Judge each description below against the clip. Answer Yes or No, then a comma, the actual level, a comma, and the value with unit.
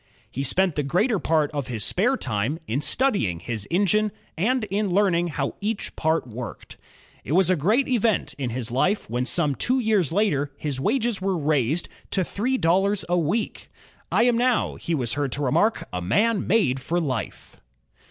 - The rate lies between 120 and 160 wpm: No, average, 180 wpm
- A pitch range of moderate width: No, wide, 7.4 semitones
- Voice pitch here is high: No, medium, 175 Hz